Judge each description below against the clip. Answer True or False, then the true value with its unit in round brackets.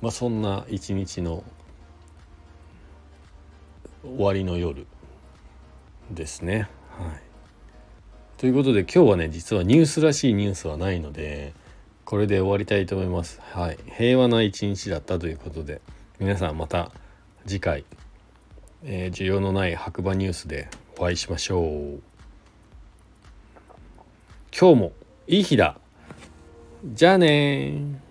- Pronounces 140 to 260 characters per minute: True (250 characters per minute)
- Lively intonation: False (4.9 semitones)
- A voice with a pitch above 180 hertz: False (90 Hz)